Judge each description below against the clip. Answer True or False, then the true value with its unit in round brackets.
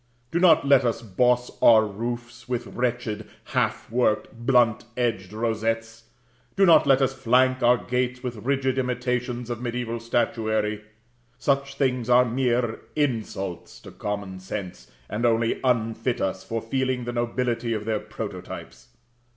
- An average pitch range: False (2.1 semitones)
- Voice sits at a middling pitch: False (120 Hz)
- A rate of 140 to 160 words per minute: True (145 wpm)